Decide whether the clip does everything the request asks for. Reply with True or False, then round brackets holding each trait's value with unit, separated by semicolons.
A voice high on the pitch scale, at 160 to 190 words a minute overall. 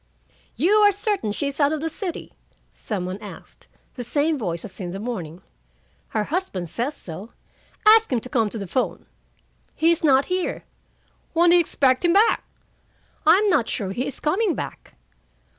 True (275 Hz; 180 wpm)